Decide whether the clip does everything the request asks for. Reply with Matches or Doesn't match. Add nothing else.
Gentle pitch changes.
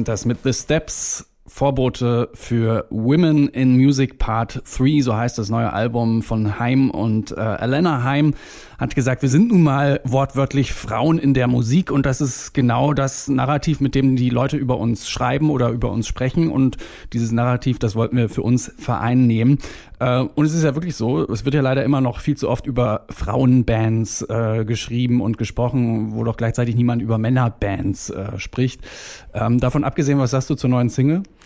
Doesn't match